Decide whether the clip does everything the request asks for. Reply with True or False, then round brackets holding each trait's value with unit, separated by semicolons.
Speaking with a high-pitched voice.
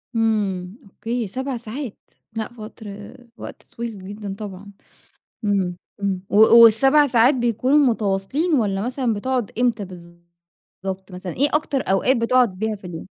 True (220 Hz)